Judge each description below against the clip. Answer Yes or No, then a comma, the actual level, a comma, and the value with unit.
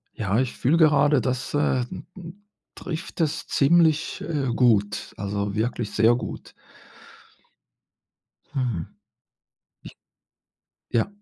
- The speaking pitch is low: Yes, low, 130 Hz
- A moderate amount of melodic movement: No, wide, 5.7 semitones